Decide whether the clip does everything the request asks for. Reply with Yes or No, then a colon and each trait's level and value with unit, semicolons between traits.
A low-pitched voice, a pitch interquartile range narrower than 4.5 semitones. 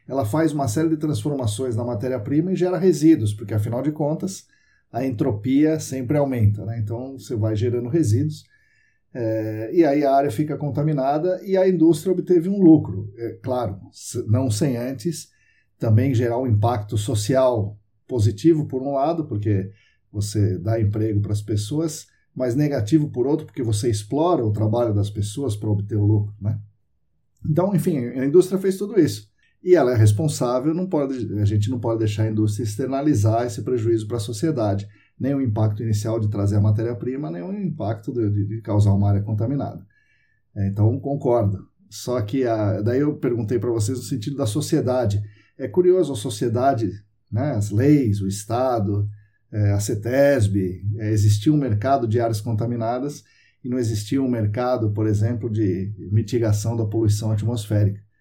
No: low, 120 Hz; average, 4.8 semitones